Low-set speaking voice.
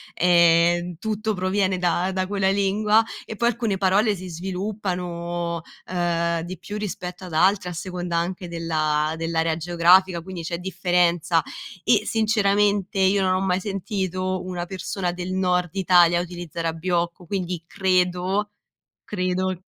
No: medium, 180 Hz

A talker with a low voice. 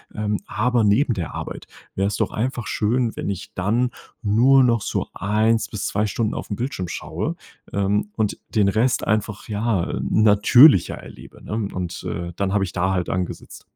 Yes: low, 105 Hz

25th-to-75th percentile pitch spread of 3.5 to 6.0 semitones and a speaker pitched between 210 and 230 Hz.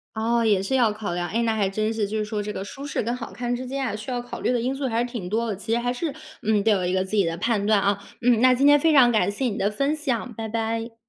No: average, 2.9 semitones; high, 225 Hz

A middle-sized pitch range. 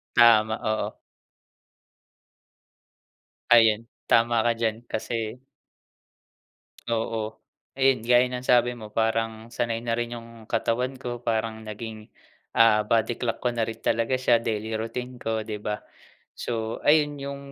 No: narrow, 1.5 semitones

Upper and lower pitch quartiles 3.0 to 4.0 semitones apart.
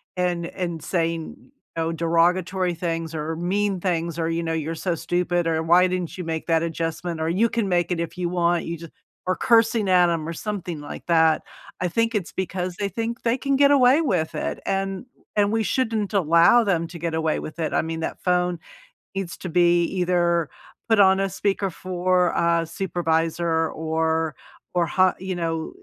No: narrow, 2.6 semitones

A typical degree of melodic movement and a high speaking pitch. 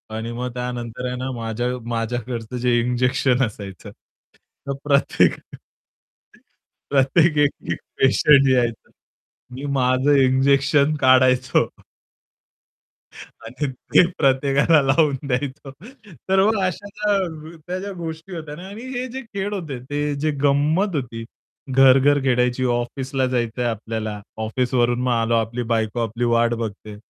No: average, 3.5 semitones; low, 130 Hz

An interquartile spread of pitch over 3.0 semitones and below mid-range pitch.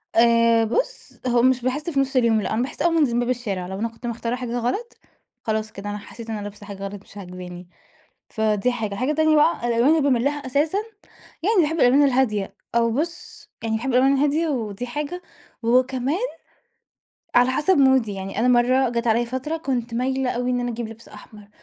No: average, 3.5 semitones; high, 245 Hz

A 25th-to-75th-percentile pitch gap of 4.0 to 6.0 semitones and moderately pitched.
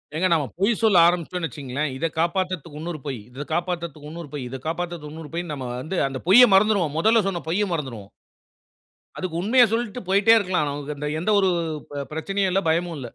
Yes: average, 4.3 semitones; medium, 170 Hz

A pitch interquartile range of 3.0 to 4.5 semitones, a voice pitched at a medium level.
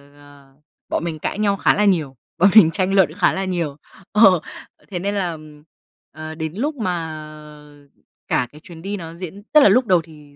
Yes: average, 4.1 semitones; medium, 175 Hz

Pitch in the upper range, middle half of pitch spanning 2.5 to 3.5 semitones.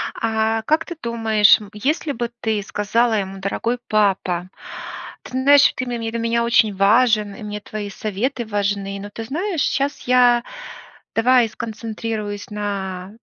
Yes: high, 220 Hz; average, 2.8 semitones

